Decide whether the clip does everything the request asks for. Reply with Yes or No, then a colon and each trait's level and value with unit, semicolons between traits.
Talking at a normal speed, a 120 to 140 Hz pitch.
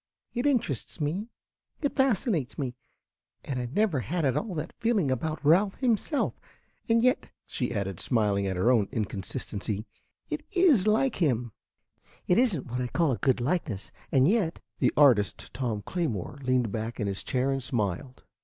Yes: average, 170 wpm; low, 135 Hz